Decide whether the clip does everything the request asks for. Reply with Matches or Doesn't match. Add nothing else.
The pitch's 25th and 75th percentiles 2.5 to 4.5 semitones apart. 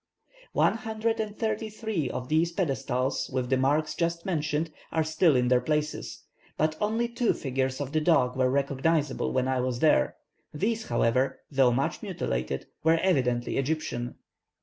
Doesn't match